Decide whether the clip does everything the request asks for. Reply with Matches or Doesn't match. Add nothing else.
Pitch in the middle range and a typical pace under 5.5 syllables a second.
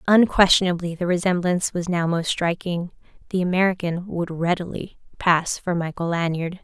Matches